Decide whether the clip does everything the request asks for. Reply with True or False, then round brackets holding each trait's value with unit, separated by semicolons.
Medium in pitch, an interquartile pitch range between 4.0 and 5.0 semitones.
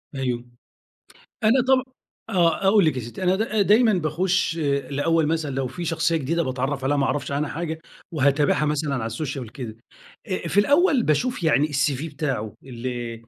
True (150 Hz; 4.6 semitones)